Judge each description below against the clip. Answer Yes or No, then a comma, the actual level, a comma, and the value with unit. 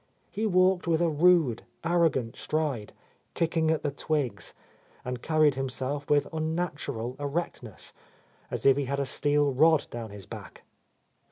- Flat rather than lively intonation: No, average, 3.7 semitones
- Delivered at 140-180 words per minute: Yes, average, 145 wpm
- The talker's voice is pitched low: No, medium, 145 Hz